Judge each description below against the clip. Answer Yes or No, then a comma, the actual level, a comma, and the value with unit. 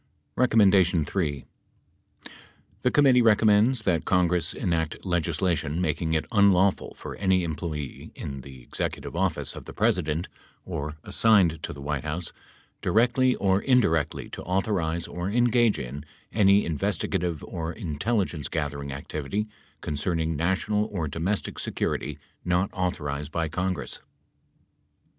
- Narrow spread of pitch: No, average, 4.6 semitones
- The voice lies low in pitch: Yes, very low, 85 Hz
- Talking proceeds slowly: Yes, slow, 120 wpm